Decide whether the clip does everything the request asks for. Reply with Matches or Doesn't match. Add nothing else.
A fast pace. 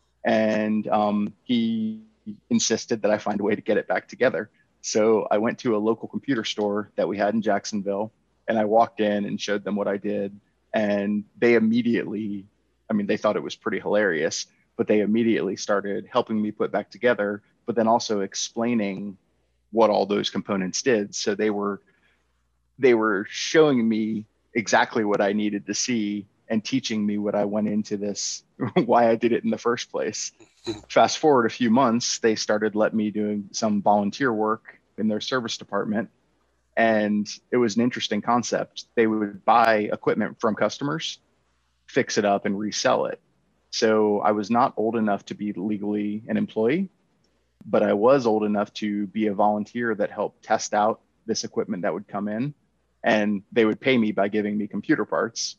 Doesn't match